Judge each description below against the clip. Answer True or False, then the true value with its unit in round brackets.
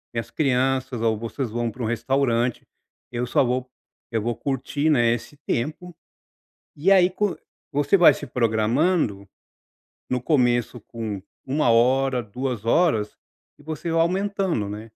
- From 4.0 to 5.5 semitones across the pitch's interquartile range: True (4.5 semitones)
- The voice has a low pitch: True (125 Hz)